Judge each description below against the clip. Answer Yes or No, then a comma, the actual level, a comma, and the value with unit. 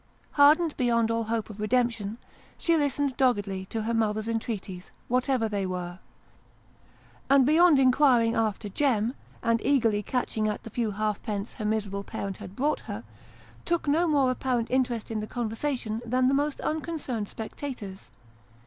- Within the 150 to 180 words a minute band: Yes, average, 155 wpm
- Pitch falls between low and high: No, high, 230 Hz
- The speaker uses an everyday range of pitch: Yes, average, 4.1 semitones